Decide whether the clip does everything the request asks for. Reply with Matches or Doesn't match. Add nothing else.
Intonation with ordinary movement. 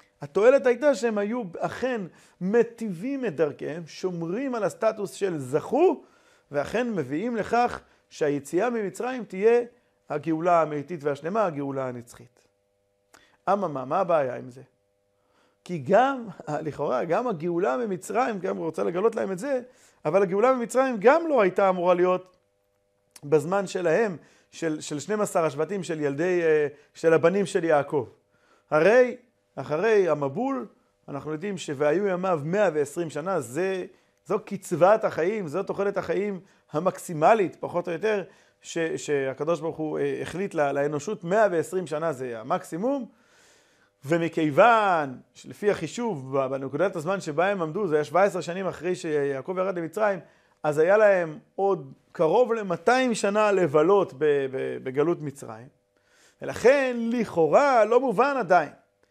Doesn't match